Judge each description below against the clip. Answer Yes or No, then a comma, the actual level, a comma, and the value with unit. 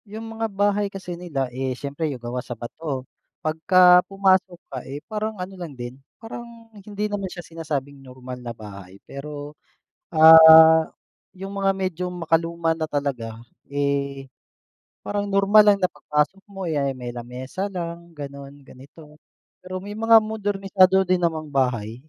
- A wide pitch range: Yes, wide, 5.9 semitones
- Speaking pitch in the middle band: Yes, medium, 165 Hz